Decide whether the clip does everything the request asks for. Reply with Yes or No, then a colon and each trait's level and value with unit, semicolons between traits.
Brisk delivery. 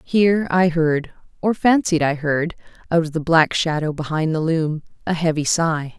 No: average, 160 wpm